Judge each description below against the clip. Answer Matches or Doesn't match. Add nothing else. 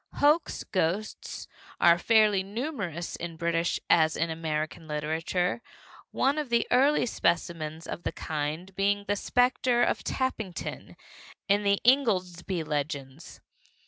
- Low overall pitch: Doesn't match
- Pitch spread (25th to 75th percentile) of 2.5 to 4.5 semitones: Doesn't match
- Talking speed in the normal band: Doesn't match